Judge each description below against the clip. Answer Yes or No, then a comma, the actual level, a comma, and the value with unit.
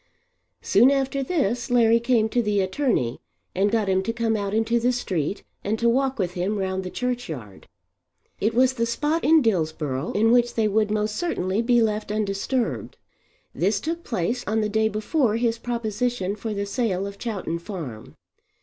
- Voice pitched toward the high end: Yes, high, 220 Hz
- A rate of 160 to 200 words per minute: Yes, average, 175 wpm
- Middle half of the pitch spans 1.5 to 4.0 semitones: Yes, average, 3.6 semitones